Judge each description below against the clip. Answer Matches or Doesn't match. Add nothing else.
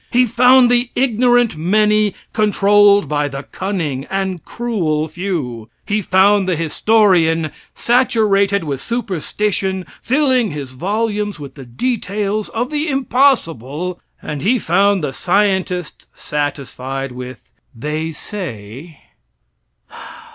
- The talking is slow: Matches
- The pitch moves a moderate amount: Doesn't match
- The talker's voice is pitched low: Doesn't match